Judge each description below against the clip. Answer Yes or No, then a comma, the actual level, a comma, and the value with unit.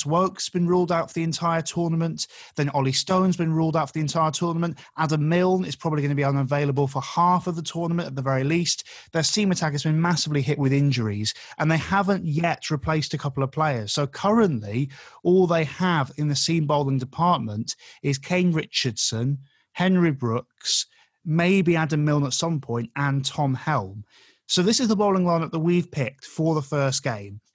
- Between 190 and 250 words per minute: Yes, average, 195 wpm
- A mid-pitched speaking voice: Yes, medium, 155 Hz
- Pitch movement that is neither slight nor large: Yes, average, 3.6 semitones